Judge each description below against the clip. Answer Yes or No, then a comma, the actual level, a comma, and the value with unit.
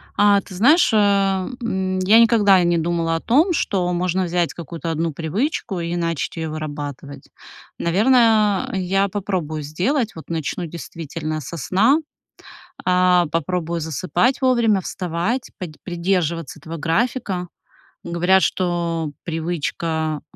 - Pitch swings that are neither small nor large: Yes, average, 3.4 semitones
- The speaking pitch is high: No, medium, 175 Hz